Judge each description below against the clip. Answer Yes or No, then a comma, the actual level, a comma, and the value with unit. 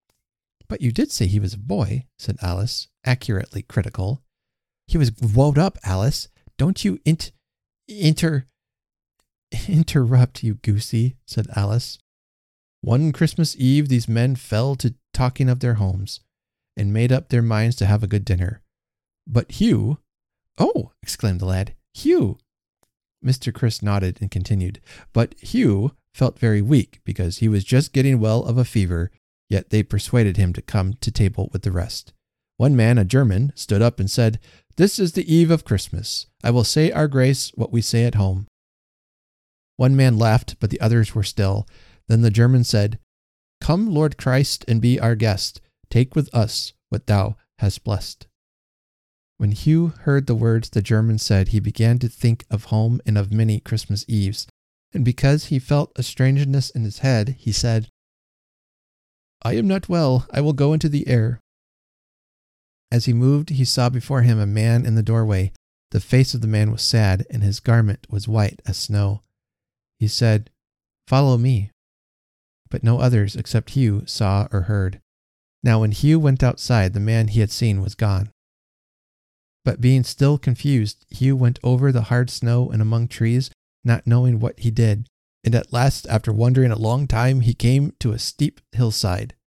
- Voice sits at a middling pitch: No, low, 115 Hz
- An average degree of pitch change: Yes, average, 3.6 semitones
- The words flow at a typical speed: Yes, average, 170 wpm